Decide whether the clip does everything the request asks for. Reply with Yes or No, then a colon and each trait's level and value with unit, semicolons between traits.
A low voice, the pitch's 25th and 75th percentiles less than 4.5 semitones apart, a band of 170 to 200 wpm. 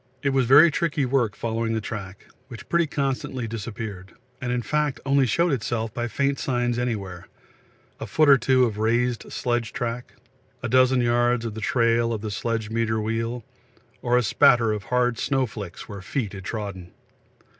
Yes: low, 120 Hz; average, 2.7 semitones; average, 175 wpm